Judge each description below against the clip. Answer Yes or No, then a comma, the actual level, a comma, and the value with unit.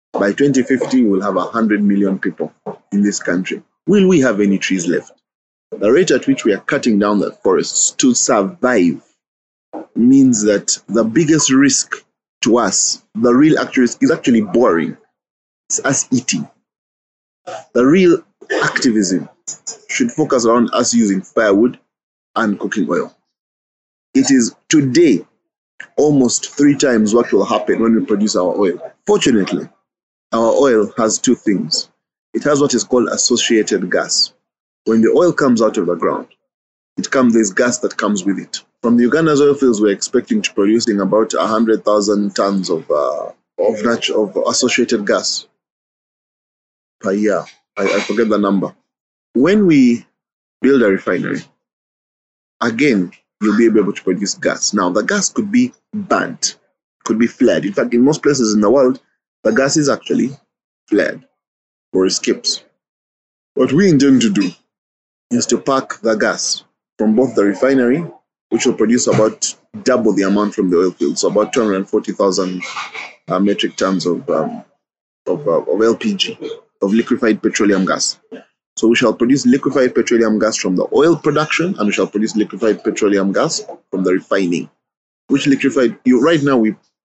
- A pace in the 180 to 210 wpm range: No, average, 160 wpm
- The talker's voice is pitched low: Yes, low, 120 Hz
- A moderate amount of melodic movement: No, wide, 8.9 semitones